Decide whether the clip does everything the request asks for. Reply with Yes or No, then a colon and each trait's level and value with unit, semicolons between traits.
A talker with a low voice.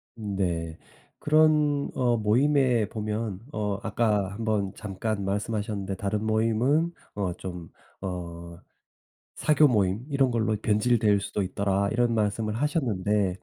Yes: low, 105 Hz